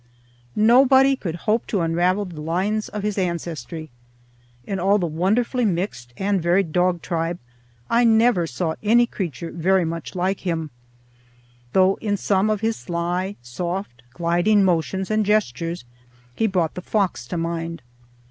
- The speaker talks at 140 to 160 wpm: Yes, average, 145 wpm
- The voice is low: No, medium, 185 Hz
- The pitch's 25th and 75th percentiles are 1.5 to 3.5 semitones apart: No, average, 3.9 semitones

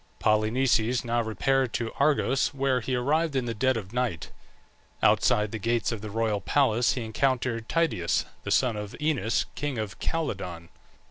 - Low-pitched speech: Yes, low, 120 Hz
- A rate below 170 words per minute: Yes, average, 160 wpm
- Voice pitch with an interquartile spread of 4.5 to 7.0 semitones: No, average, 3.7 semitones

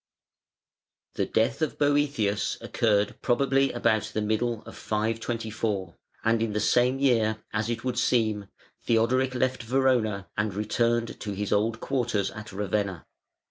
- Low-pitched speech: Yes, low, 110 Hz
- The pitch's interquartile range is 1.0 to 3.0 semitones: Yes, narrow, 2.6 semitones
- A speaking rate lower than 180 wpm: Yes, average, 140 wpm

